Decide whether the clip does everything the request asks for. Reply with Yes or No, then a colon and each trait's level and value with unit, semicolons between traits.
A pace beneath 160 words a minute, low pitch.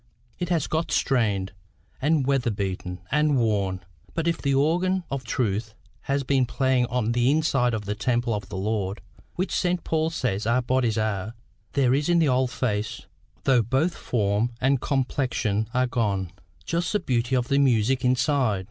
No: average, 165 wpm; low, 125 Hz